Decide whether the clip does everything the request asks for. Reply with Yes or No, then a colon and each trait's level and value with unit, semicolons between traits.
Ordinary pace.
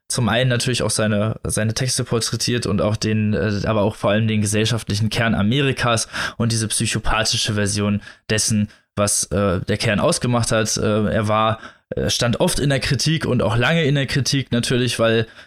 Yes: average, 180 wpm